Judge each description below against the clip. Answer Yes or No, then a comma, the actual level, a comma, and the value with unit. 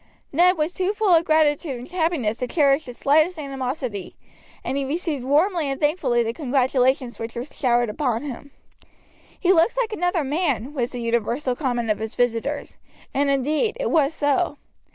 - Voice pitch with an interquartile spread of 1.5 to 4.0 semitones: No, average, 4.5 semitones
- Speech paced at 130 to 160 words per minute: No, average, 170 wpm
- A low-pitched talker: No, very high, 280 Hz